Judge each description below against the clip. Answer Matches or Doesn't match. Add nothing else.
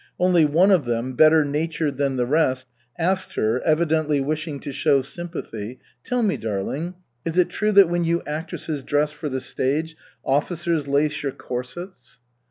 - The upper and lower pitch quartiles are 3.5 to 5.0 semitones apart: Matches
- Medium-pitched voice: Matches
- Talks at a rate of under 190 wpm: Matches